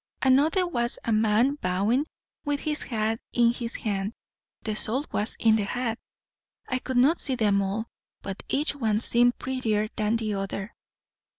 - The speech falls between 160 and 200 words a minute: Yes, average, 165 wpm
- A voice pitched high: Yes, high, 230 Hz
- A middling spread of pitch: Yes, average, 3.4 semitones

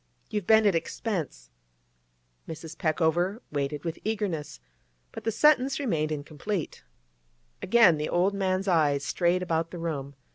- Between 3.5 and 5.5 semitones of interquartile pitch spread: Yes, average, 4.7 semitones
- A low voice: No, medium, 170 Hz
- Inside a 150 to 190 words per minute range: No, slow, 135 wpm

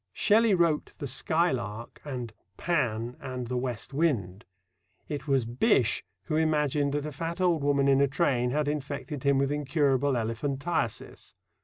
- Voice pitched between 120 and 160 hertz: Yes, medium, 140 Hz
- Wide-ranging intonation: No, average, 3.5 semitones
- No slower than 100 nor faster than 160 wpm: Yes, average, 150 wpm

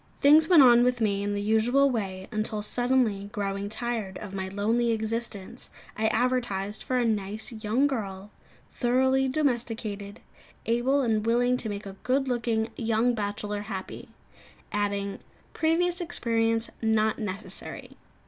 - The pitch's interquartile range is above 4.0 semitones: No, average, 3.2 semitones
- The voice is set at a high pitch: Yes, high, 225 Hz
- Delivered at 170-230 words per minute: No, average, 140 wpm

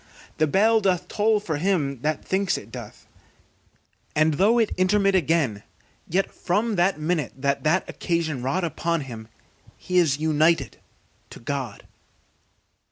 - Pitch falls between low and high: Yes, medium, 165 Hz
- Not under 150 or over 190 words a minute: No, average, 140 wpm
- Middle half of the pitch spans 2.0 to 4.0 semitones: No, average, 5.2 semitones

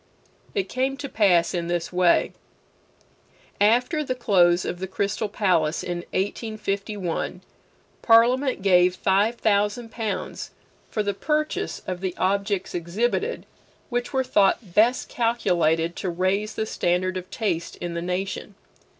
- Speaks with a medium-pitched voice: No, high, 200 Hz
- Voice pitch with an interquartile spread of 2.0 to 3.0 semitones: No, average, 4.2 semitones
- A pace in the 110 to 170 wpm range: Yes, slow, 135 wpm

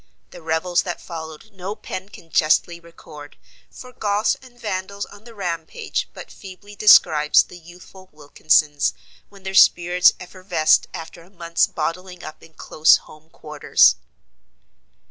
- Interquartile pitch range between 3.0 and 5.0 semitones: Yes, average, 3.5 semitones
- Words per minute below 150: Yes, average, 140 wpm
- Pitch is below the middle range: No, medium, 175 Hz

